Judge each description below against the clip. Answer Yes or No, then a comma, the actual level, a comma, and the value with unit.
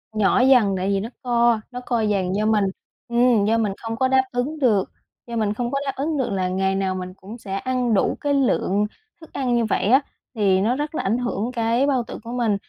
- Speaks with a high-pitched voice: Yes, high, 230 Hz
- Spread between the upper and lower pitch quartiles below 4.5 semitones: Yes, average, 3.9 semitones